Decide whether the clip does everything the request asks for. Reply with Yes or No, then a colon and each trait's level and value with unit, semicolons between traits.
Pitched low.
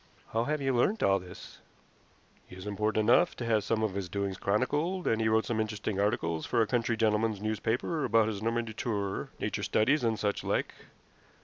Yes: low, 110 Hz